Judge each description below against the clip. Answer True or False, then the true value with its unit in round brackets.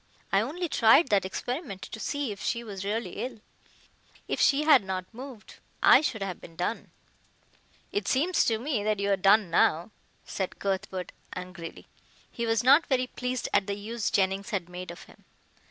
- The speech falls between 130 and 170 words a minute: False (180 wpm)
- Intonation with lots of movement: False (4.8 semitones)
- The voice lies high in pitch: True (215 Hz)